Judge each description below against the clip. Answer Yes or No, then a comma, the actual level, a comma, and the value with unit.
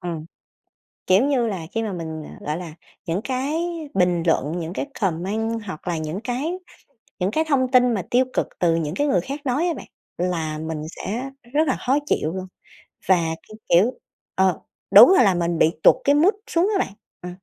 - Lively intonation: Yes, wide, 7.2 semitones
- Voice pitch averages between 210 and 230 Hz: No, high, 190 Hz